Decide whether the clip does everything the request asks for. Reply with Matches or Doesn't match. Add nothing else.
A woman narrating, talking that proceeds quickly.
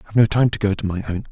Doesn't match